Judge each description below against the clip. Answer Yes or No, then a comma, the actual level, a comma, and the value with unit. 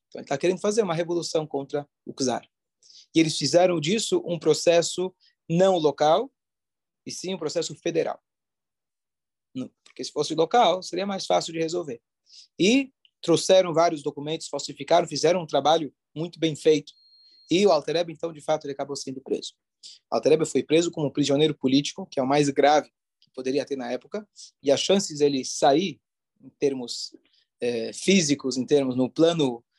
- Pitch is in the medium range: Yes, medium, 155 Hz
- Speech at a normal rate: Yes, average, 165 wpm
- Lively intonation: No, average, 3.5 semitones